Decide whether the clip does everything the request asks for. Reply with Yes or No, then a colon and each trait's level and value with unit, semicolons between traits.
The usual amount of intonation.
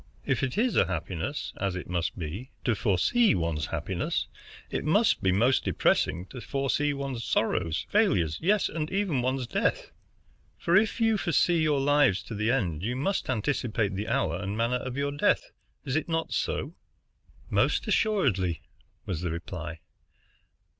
No: wide, 8.2 semitones